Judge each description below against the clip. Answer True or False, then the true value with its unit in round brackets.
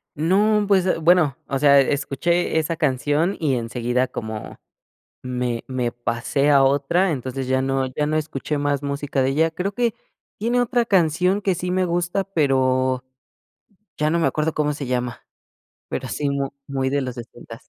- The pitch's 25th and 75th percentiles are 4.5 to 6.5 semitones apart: True (4.8 semitones)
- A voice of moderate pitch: True (145 Hz)